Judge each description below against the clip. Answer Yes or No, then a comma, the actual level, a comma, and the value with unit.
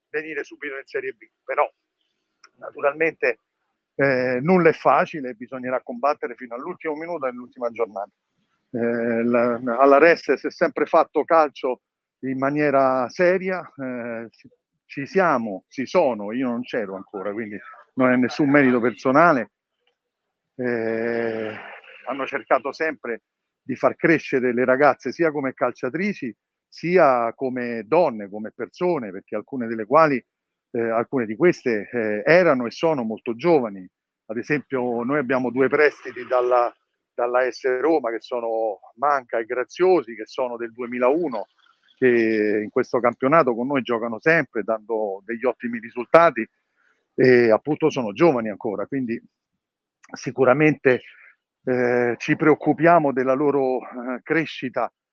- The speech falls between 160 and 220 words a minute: No, average, 130 wpm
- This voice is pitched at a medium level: No, low, 130 Hz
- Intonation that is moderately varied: Yes, average, 4.4 semitones